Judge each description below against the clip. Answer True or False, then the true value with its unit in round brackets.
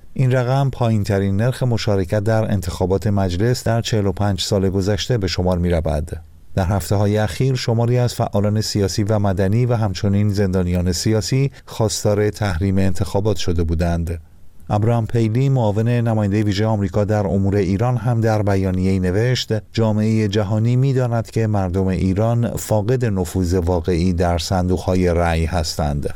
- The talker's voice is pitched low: True (105 Hz)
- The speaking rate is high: False (145 wpm)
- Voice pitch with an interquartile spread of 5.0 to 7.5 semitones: False (3.3 semitones)